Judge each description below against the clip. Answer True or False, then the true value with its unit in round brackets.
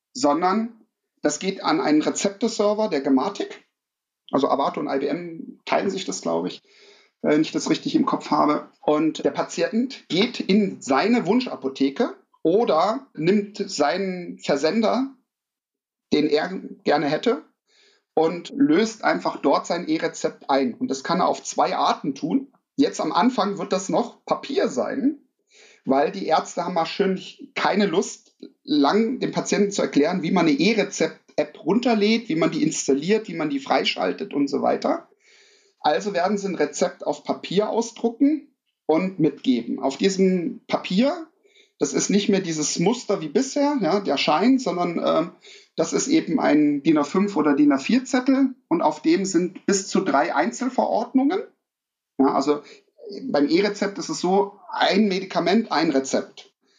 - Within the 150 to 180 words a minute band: True (155 wpm)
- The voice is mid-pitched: False (215 Hz)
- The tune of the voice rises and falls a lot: True (8.3 semitones)